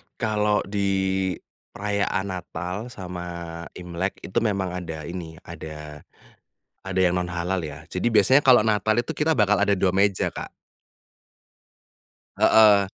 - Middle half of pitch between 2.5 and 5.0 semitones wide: Yes, average, 3.0 semitones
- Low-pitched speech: Yes, very low, 95 Hz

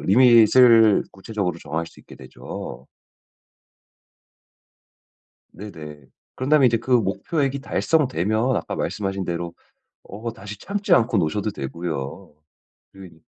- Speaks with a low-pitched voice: Yes, low, 105 Hz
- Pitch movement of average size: No, wide, 6.4 semitones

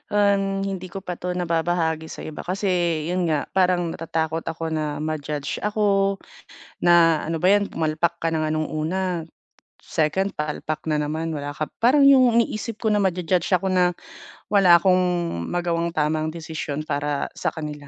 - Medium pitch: Yes, medium, 165 Hz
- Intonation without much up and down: No, average, 3.1 semitones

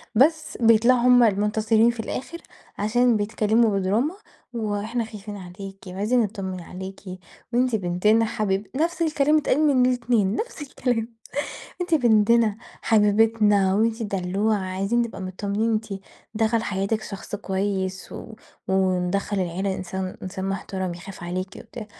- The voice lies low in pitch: No, high, 210 Hz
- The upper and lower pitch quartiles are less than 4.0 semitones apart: Yes, average, 3.4 semitones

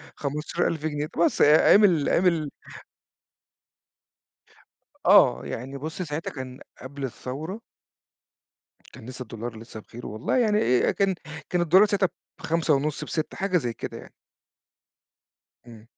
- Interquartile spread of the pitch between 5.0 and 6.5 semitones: Yes, wide, 5.5 semitones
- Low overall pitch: No, medium, 150 Hz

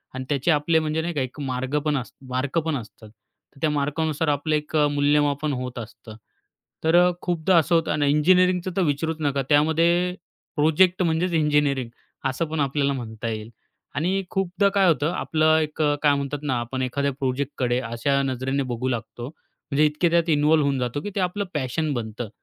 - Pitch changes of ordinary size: Yes, average, 3.4 semitones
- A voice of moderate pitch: Yes, medium, 145 Hz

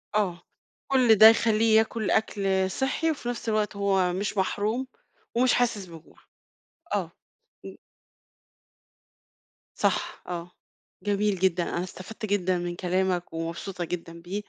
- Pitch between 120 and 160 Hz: No, high, 195 Hz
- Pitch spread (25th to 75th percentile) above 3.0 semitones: Yes, average, 3.5 semitones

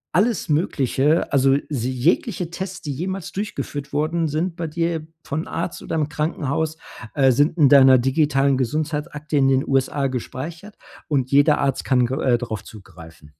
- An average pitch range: Yes, average, 3.5 semitones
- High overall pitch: No, medium, 145 Hz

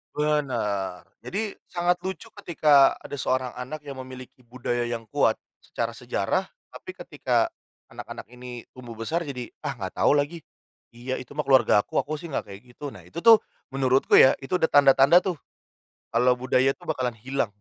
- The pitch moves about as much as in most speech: Yes, average, 3.4 semitones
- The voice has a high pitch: No, low, 130 Hz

